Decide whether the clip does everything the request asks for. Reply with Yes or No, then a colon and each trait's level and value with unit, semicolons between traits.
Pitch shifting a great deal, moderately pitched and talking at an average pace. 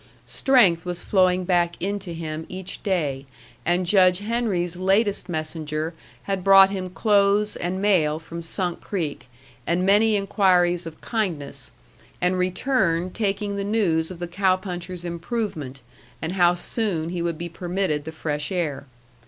No: average, 2.9 semitones; medium, 180 Hz; average, 145 wpm